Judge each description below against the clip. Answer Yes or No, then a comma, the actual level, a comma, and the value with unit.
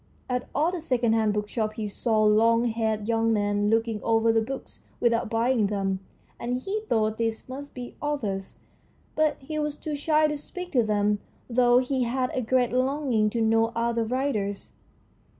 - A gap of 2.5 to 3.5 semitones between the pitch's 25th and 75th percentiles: Yes, average, 3.2 semitones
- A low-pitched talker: No, high, 230 Hz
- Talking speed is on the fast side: No, average, 175 wpm